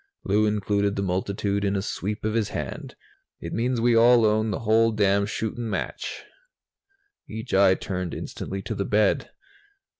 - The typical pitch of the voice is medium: No, low, 105 Hz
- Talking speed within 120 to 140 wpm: No, average, 160 wpm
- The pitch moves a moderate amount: No, narrow, 2.0 semitones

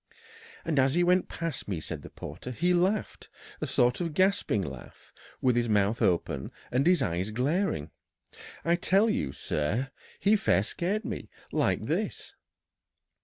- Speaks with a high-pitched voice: No, low, 135 Hz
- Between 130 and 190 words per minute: Yes, average, 155 wpm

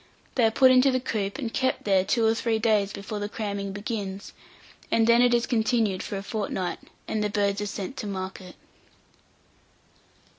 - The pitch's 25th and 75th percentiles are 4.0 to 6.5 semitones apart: No, average, 2.7 semitones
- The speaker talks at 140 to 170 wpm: No, average, 185 wpm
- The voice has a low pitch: No, high, 210 Hz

